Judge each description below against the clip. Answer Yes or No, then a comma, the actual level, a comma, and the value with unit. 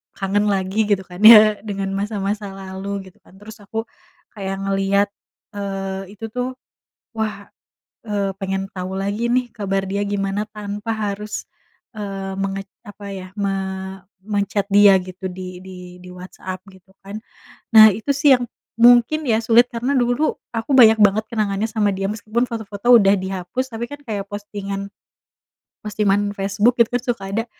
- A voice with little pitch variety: Yes, narrow, 2.3 semitones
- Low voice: No, high, 205 Hz